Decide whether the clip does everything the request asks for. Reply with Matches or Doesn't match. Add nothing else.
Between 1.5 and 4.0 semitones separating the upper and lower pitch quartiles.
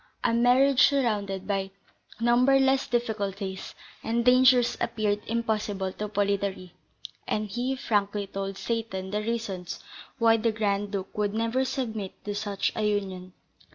Matches